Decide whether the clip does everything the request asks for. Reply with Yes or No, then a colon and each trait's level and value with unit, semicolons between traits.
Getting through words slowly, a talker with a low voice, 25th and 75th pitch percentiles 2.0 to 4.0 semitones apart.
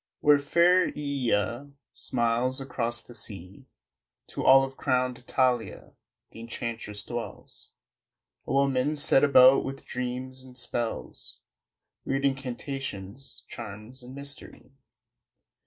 Yes: slow, 105 wpm; low, 130 Hz; narrow, 2.4 semitones